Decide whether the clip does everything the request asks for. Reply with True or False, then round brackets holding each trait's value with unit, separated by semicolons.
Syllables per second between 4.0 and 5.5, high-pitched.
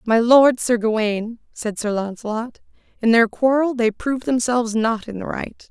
True (4.9 syllables/s; 230 Hz)